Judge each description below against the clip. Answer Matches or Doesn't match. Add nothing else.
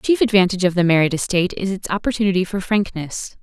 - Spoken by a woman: Matches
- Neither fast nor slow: Doesn't match